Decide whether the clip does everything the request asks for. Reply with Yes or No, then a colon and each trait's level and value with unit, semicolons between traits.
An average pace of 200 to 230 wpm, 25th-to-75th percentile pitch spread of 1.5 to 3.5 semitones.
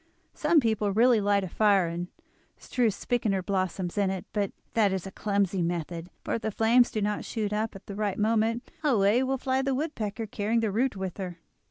Yes: fast, 205 wpm; average, 3.0 semitones